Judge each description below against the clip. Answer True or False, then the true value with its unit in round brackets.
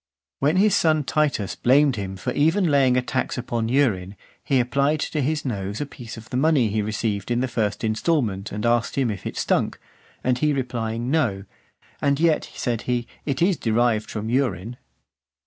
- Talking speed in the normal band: True (185 wpm)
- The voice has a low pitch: True (125 Hz)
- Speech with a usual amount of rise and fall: True (4.5 semitones)